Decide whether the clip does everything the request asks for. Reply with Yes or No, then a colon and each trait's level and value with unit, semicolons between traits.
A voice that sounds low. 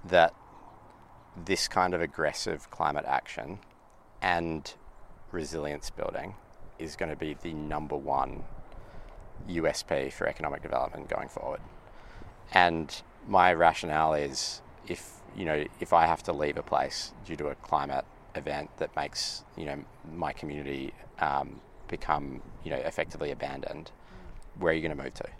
Yes: very low, 80 Hz